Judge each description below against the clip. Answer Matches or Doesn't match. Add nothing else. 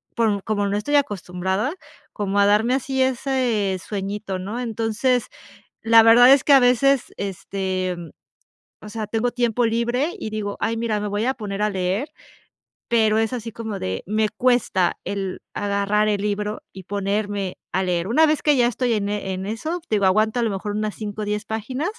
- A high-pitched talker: Matches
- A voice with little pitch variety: Doesn't match